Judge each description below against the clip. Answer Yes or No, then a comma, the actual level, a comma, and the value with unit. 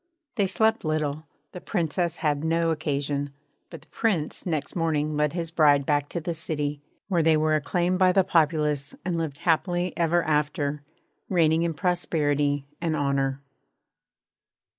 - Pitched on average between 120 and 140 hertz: No, medium, 155 Hz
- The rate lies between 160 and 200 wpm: No, average, 150 wpm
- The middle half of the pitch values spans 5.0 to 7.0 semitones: No, average, 2.7 semitones